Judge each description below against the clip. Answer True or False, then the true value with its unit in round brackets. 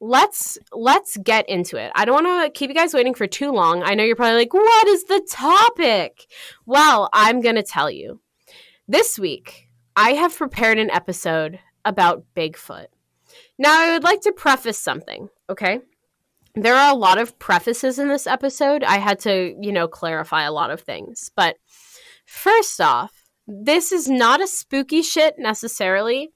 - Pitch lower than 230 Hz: False (265 Hz)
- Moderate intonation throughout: False (8.0 semitones)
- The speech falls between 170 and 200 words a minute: True (175 wpm)